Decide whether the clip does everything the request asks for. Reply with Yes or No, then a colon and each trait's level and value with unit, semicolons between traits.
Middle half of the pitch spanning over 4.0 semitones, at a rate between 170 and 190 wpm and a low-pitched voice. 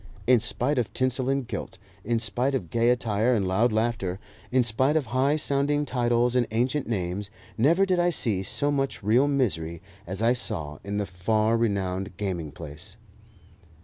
Yes: average, 4.8 semitones; average, 175 wpm; low, 115 Hz